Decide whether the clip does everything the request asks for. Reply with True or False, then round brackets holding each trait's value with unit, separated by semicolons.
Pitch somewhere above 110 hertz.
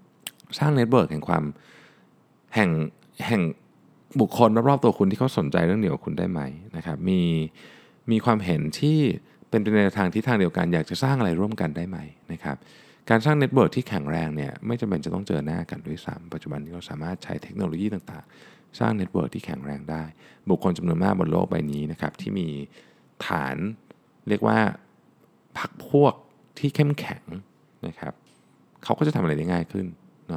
False (105 Hz)